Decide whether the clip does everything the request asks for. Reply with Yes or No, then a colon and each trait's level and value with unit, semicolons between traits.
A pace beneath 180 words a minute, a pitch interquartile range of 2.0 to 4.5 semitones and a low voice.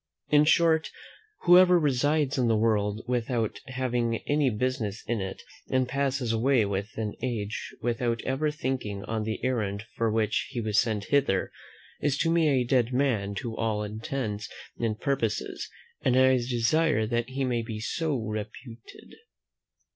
Yes: average, 150 wpm; average, 3.6 semitones; low, 120 Hz